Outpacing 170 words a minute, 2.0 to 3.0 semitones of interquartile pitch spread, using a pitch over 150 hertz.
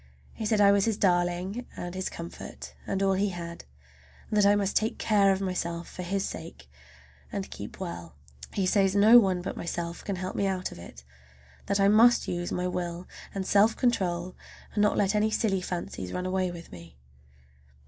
Yes: average, 195 wpm; narrow, 2.5 semitones; high, 190 Hz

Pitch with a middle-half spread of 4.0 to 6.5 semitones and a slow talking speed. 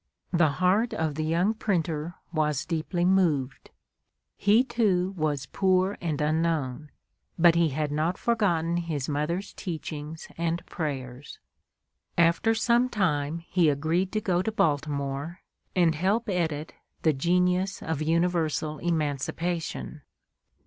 No: average, 3.3 semitones; slow, 120 wpm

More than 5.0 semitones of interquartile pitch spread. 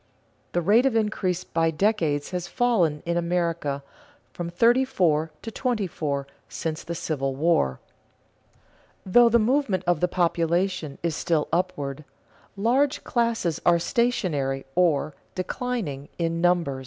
Yes: wide, 5.6 semitones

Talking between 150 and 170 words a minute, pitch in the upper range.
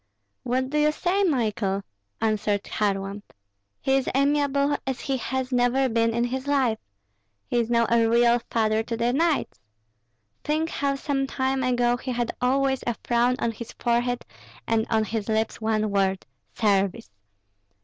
Yes: average, 160 wpm; high, 240 Hz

